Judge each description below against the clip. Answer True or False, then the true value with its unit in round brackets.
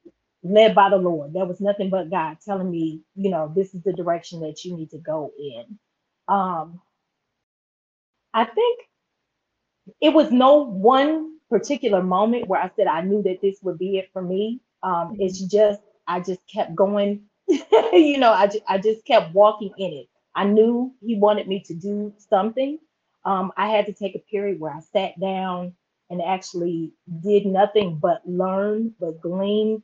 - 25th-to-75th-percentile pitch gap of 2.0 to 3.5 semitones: True (3.0 semitones)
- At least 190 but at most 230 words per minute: False (175 wpm)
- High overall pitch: True (195 Hz)